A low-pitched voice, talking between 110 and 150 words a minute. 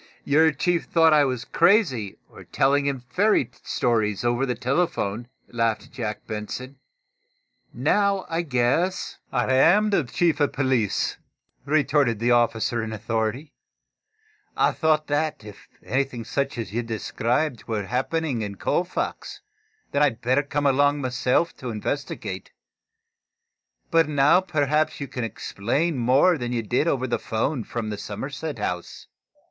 Yes: low, 130 Hz; average, 145 wpm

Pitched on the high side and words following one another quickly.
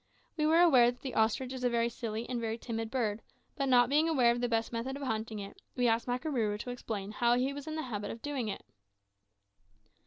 Yes: high, 240 Hz; fast, 235 wpm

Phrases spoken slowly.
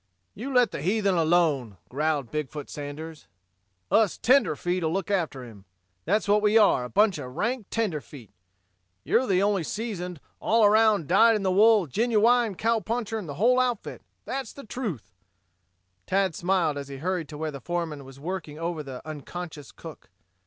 No: average, 165 wpm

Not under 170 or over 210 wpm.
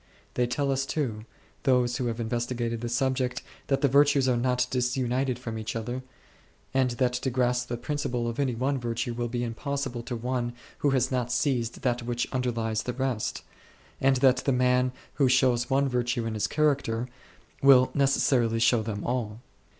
Yes: average, 180 wpm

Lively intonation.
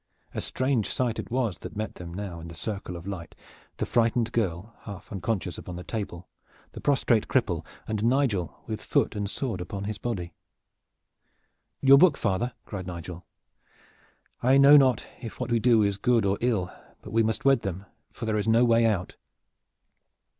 No: average, 4.2 semitones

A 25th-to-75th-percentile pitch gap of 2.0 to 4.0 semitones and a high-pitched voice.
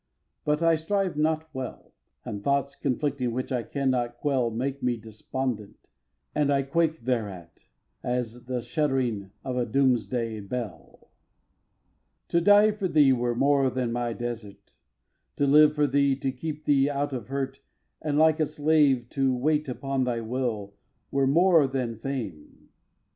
No: average, 3.5 semitones; low, 135 Hz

